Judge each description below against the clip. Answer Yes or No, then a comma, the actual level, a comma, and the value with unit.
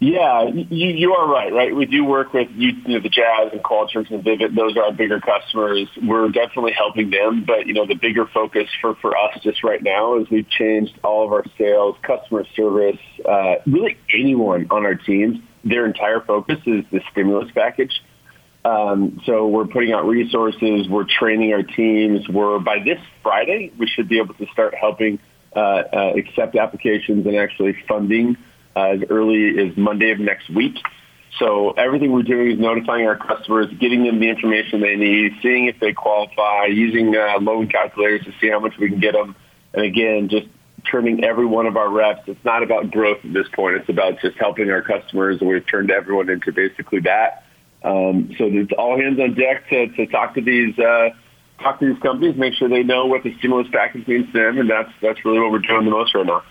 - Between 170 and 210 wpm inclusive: Yes, fast, 205 wpm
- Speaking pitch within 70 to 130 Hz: Yes, low, 110 Hz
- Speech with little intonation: Yes, narrow, 2.2 semitones